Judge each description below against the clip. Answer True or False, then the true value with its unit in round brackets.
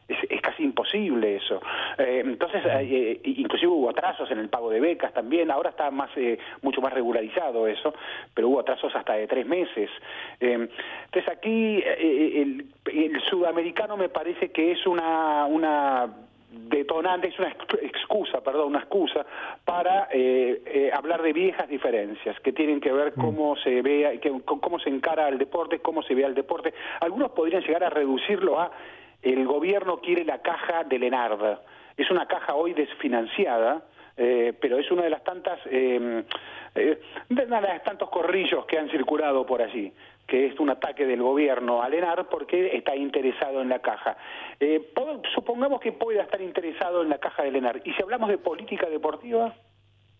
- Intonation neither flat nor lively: False (6.5 semitones)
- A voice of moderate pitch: True (165 Hz)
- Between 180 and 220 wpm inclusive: False (170 wpm)